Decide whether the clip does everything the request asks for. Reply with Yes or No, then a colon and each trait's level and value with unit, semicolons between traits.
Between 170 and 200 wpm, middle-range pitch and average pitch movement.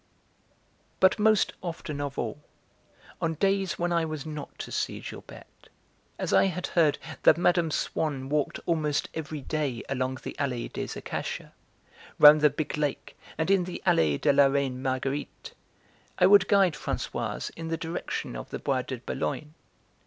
No: average, 160 wpm; medium, 150 Hz; average, 3.9 semitones